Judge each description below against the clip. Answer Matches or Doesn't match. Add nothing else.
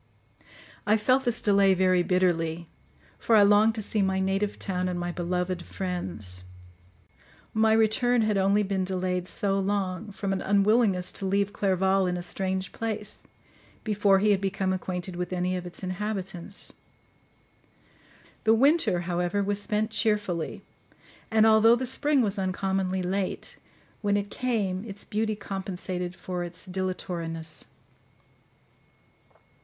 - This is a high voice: Matches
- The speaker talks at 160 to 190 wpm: Doesn't match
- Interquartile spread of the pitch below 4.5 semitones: Matches